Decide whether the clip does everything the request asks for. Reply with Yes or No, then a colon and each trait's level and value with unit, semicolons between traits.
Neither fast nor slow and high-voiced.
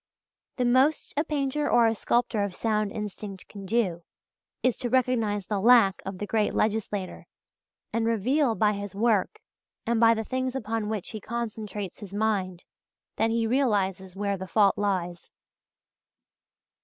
Yes: average, 155 wpm; high, 215 Hz